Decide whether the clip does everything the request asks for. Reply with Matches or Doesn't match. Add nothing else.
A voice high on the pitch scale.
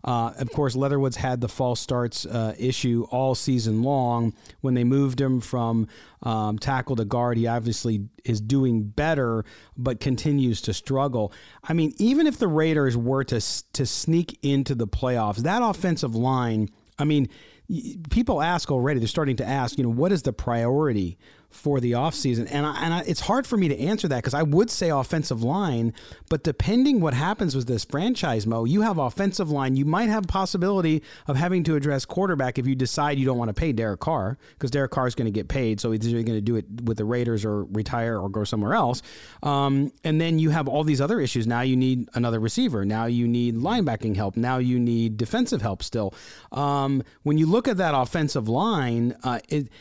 Doesn't match